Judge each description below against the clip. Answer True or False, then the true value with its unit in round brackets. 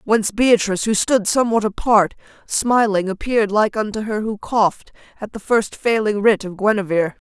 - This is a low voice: False (210 Hz)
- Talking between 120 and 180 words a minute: True (165 wpm)